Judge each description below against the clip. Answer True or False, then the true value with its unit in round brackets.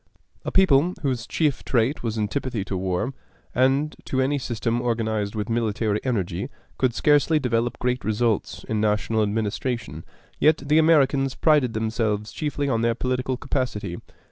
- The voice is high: False (120 Hz)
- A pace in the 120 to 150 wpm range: True (145 wpm)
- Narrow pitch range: False (3.8 semitones)